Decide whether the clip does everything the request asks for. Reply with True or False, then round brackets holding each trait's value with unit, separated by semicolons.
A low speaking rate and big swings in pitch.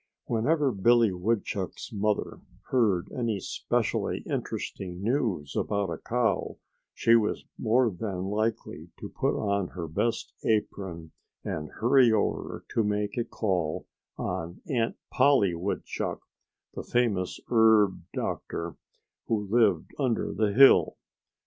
False (120 wpm; 3.9 semitones)